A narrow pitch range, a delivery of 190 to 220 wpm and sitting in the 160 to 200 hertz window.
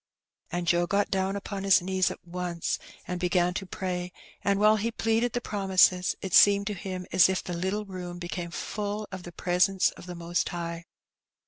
Yes: narrow, 2.1 semitones; average, 195 wpm; medium, 185 Hz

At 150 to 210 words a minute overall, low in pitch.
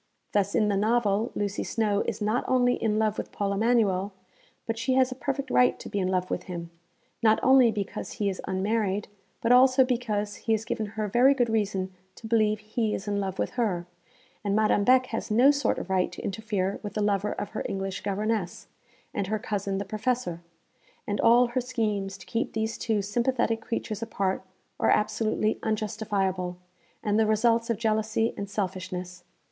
No: average, 190 wpm; high, 215 Hz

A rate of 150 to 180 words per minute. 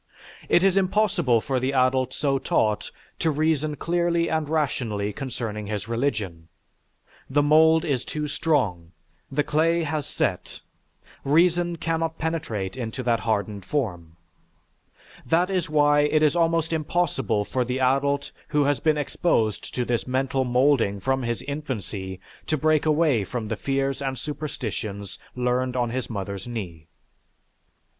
No: average, 140 wpm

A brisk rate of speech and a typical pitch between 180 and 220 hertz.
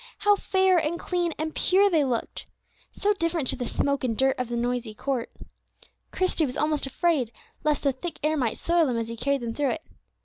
No: fast, 210 wpm; very high, 290 Hz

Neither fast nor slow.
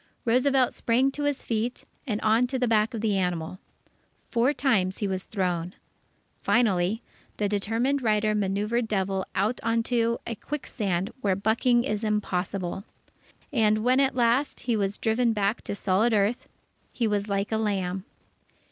Yes: average, 155 wpm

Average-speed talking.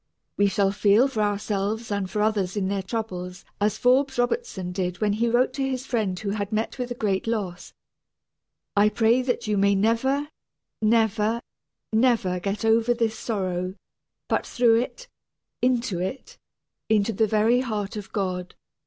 Yes: average, 160 wpm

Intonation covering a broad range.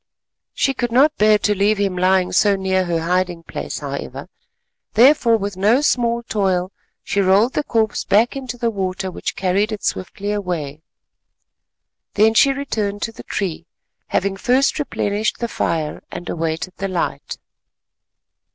No: average, 3.8 semitones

